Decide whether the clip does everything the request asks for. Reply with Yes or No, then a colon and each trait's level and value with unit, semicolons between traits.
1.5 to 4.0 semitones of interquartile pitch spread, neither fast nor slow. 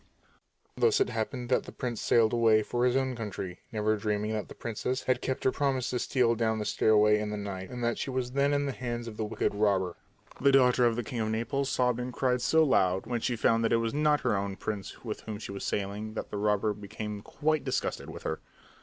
No: average, 3.2 semitones; fast, 240 wpm